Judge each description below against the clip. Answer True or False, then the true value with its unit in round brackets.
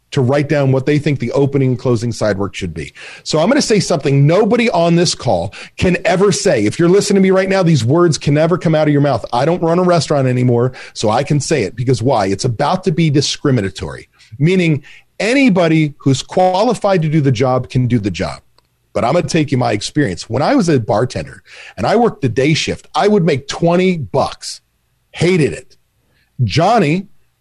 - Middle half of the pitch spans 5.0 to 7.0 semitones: True (5.3 semitones)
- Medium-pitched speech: True (150 Hz)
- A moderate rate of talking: False (220 wpm)